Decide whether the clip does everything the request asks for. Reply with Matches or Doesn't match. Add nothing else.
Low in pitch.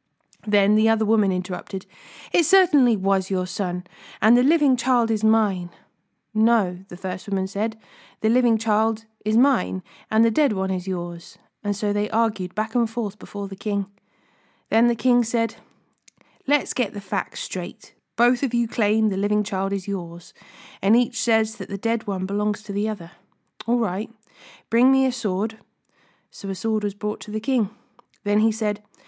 Doesn't match